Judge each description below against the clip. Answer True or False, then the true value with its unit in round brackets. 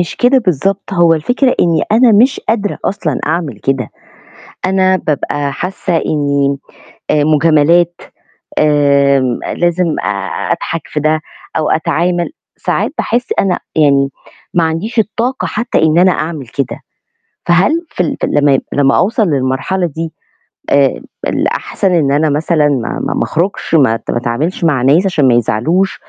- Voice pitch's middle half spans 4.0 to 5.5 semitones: True (4.8 semitones)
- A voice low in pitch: False (160 Hz)